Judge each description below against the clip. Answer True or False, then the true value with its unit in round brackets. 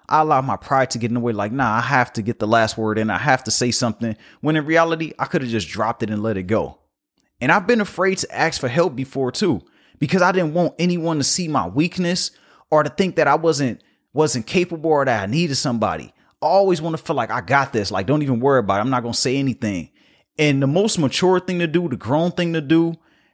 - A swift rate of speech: True (260 wpm)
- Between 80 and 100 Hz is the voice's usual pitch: False (140 Hz)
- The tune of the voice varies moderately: False (5.8 semitones)